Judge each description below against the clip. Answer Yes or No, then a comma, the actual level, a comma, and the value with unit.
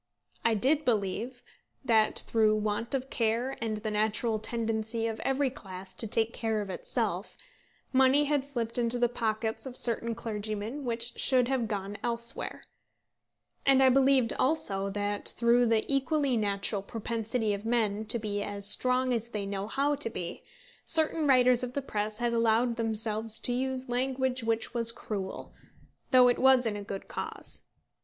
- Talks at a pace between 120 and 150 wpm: No, average, 165 wpm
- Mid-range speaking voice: No, high, 230 Hz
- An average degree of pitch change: Yes, average, 3.0 semitones